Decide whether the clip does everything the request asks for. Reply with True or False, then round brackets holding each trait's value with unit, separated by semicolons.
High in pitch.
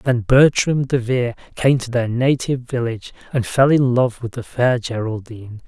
False (125 Hz)